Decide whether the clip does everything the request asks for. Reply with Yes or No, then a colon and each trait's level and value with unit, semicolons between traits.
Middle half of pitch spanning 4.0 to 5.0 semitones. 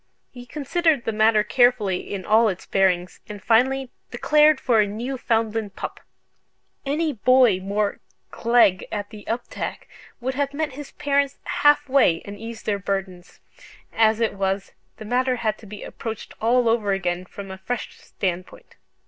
Yes: average, 4.3 semitones